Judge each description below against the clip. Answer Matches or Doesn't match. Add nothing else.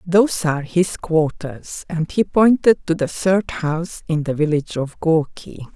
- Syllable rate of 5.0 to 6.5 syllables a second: Doesn't match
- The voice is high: Doesn't match